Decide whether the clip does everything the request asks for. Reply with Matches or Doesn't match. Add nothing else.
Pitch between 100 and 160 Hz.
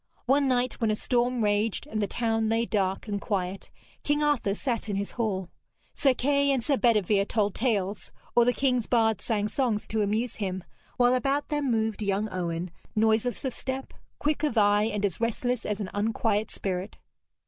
Doesn't match